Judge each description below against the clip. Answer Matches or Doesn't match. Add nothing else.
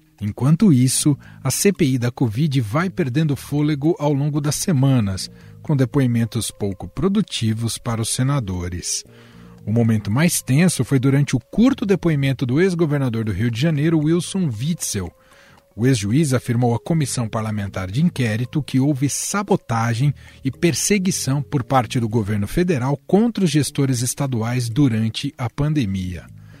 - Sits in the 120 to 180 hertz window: Matches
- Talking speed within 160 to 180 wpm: Doesn't match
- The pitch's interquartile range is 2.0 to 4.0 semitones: Doesn't match